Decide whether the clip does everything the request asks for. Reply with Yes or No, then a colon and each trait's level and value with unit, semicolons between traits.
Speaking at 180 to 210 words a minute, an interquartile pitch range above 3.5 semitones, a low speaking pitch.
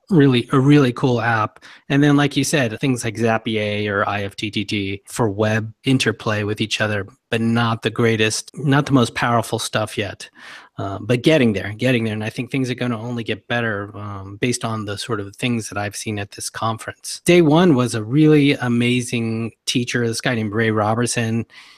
No: average, 200 wpm; average, 2.7 semitones; low, 115 Hz